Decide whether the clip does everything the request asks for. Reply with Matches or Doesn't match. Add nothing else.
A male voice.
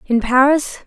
Doesn't match